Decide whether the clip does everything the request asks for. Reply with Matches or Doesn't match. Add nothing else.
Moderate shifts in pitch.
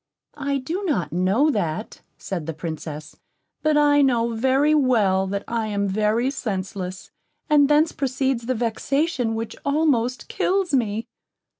Doesn't match